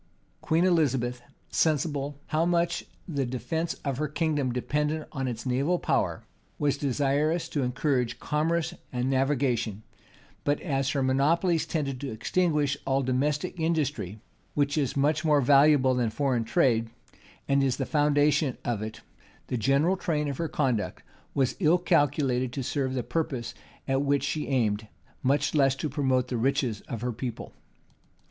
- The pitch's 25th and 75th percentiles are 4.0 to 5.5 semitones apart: No, average, 3.1 semitones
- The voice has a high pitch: No, medium, 140 Hz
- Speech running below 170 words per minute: Yes, average, 155 wpm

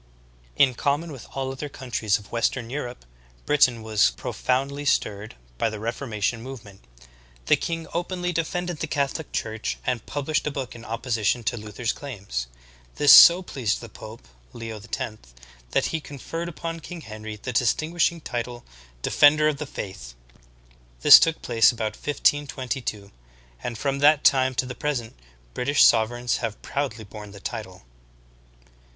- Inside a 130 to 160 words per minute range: Yes, average, 150 wpm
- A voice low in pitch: Yes, low, 125 Hz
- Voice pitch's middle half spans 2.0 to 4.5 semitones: No, average, 4.9 semitones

